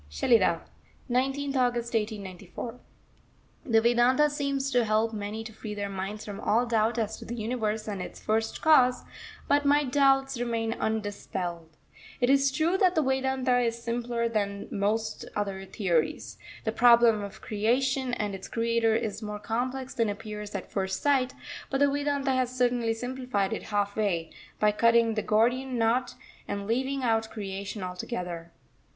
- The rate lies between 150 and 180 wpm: Yes, average, 160 wpm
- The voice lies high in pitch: Yes, high, 230 Hz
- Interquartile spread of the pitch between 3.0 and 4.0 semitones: Yes, average, 3.4 semitones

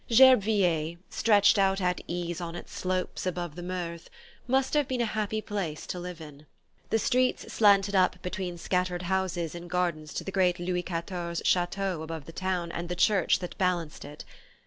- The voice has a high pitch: No, medium, 180 Hz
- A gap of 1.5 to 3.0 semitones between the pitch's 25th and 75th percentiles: Yes, narrow, 2.4 semitones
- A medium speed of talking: Yes, average, 180 wpm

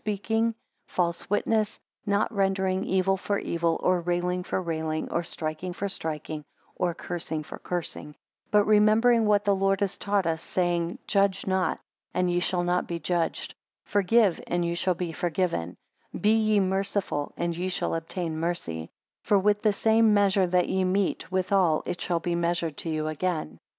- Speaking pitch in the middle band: Yes, medium, 180 Hz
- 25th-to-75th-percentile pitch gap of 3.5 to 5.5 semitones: No, average, 2.8 semitones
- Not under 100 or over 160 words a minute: No, average, 170 wpm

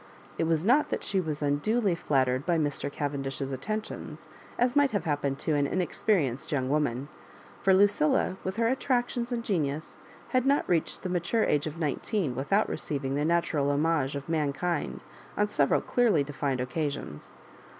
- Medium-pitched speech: Yes, medium, 155 Hz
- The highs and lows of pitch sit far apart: Yes, wide, 6.3 semitones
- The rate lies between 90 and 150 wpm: No, average, 160 wpm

